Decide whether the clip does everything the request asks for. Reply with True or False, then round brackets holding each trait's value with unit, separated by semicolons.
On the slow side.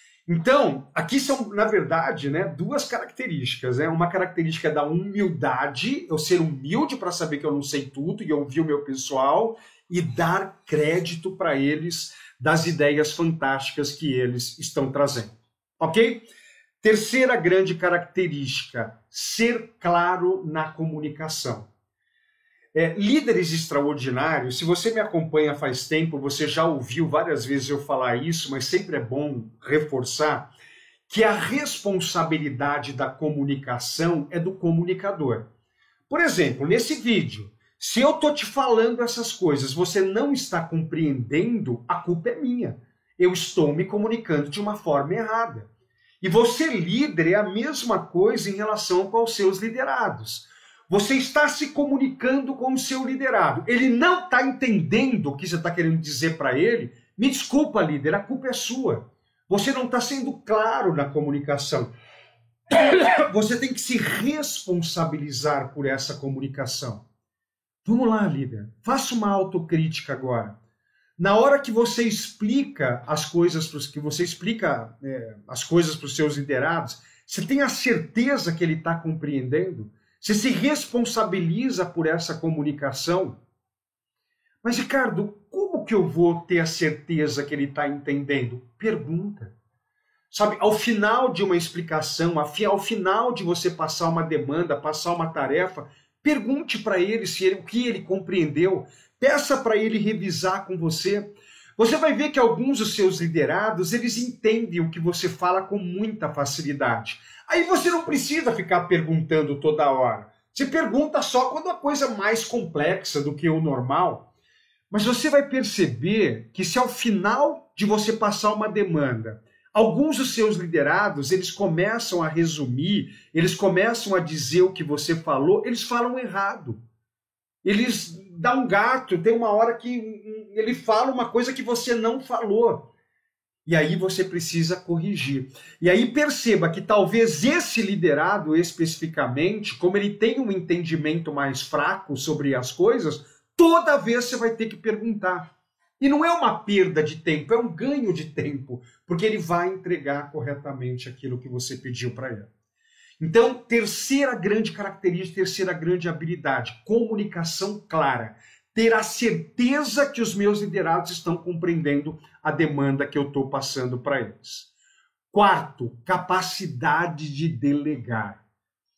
False (145 wpm)